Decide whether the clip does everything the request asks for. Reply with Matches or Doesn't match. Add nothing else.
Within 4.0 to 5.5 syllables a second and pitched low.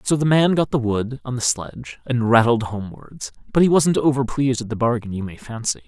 Doesn't match